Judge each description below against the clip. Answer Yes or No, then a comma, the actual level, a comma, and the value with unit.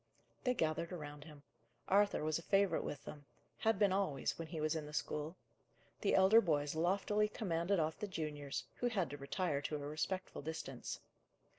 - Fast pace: No, average, 180 wpm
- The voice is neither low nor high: Yes, medium, 160 Hz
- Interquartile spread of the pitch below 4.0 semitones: No, average, 4.6 semitones